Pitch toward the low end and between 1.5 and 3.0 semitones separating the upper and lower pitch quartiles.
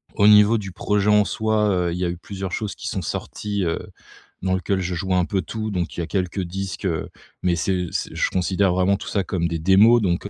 Yes: very low, 95 Hz; narrow, 2.4 semitones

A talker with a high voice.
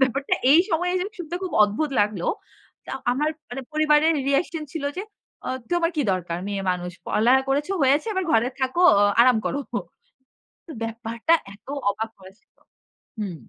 Yes: very high, 265 Hz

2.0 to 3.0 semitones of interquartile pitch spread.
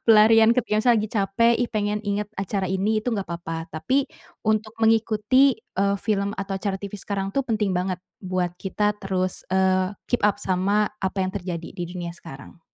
Yes: narrow, 2.5 semitones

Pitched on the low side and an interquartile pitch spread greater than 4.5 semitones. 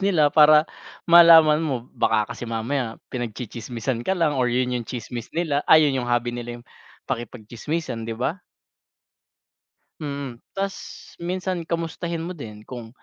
Yes: low, 130 Hz; wide, 5.5 semitones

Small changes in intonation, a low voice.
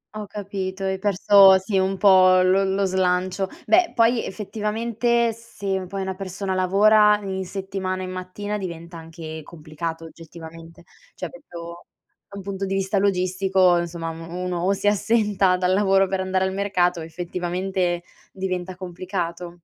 No: narrow, 1.9 semitones; high, 190 Hz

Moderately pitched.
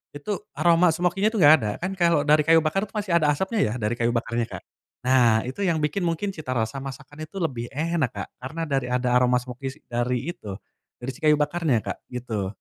Yes: medium, 145 Hz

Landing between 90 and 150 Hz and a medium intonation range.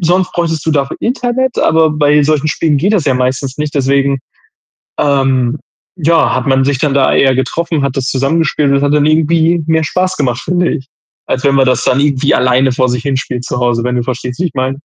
Yes: medium, 140 Hz; average, 3.5 semitones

